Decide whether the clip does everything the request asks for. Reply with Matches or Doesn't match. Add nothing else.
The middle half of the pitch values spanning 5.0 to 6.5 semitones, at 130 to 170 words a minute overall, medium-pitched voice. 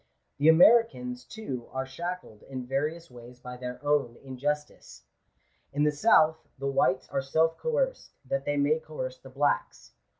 Doesn't match